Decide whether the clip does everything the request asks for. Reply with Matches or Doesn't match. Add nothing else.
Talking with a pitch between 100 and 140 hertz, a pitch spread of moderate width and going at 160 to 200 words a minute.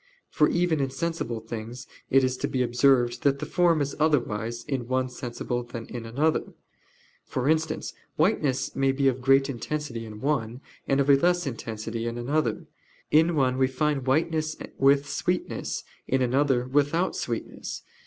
Matches